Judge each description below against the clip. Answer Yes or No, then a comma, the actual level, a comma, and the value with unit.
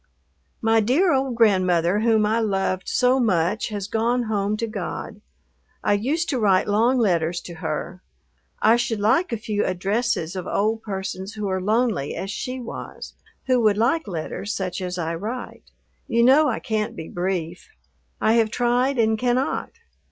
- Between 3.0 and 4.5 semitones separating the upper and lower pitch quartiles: Yes, average, 3.9 semitones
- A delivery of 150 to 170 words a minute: Yes, average, 165 wpm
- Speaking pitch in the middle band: No, high, 215 Hz